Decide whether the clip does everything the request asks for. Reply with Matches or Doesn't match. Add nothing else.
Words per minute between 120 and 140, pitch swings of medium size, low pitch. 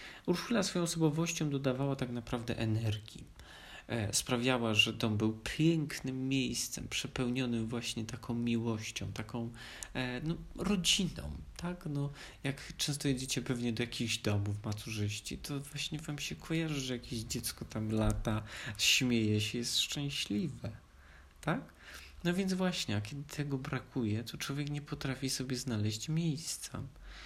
Matches